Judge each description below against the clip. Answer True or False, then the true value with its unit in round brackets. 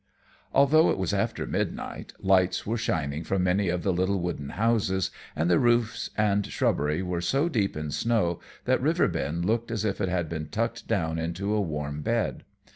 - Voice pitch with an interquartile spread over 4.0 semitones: True (4.5 semitones)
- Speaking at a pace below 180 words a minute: False (185 wpm)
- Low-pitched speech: True (95 Hz)